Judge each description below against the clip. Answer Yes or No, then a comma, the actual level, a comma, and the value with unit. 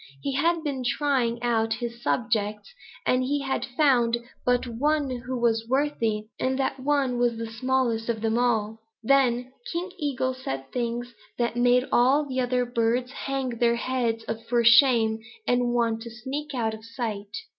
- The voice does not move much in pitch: Yes, narrow, 2.3 semitones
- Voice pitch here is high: Yes, high, 245 Hz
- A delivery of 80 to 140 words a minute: No, average, 165 wpm